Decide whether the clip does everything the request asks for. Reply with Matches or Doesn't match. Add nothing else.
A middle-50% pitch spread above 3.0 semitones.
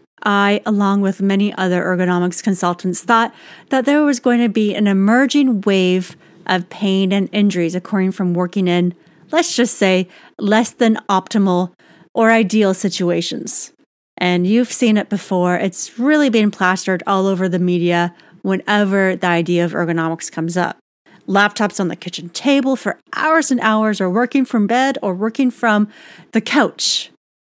Matches